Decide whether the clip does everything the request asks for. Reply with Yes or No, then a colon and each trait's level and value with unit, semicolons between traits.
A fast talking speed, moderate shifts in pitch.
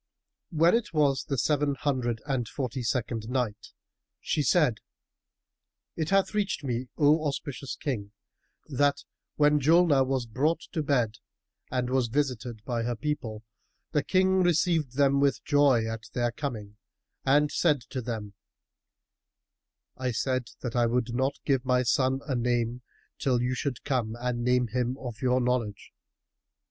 No: average, 150 wpm; average, 3.3 semitones